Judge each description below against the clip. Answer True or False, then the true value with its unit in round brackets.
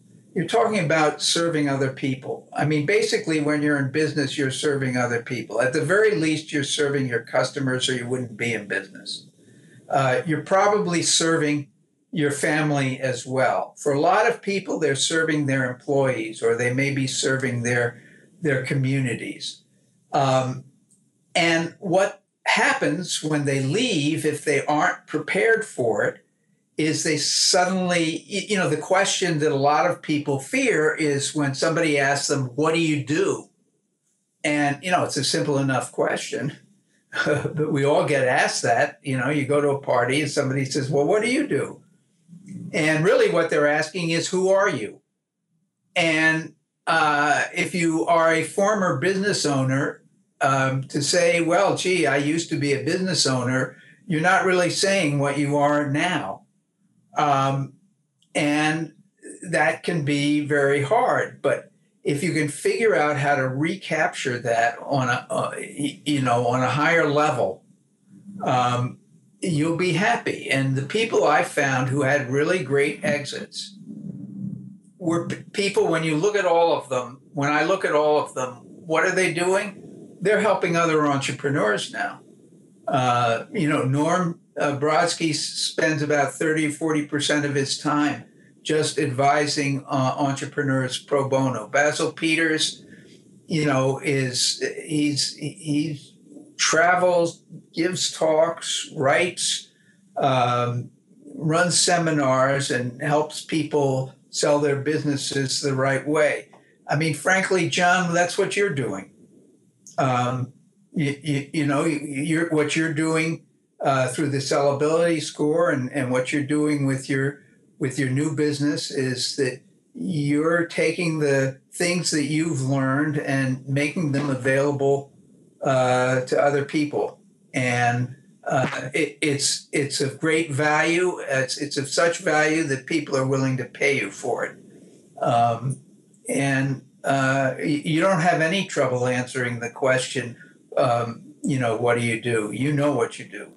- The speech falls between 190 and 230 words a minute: False (150 wpm)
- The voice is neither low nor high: True (150 Hz)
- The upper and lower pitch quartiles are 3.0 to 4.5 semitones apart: True (3.5 semitones)